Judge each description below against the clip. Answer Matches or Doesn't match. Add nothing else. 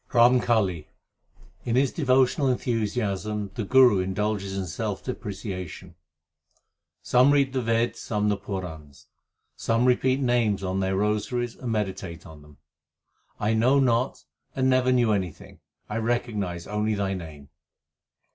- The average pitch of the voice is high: Doesn't match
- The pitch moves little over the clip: Doesn't match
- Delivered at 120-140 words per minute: Matches